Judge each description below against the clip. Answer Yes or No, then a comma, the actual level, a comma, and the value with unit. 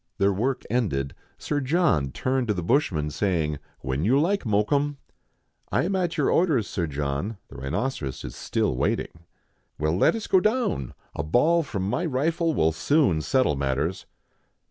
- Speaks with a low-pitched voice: Yes, low, 105 Hz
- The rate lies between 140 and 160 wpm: No, average, 175 wpm